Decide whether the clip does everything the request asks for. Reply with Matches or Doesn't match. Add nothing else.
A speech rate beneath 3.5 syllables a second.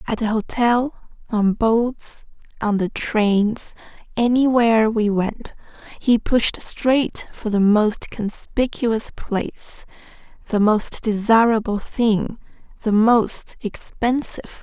Matches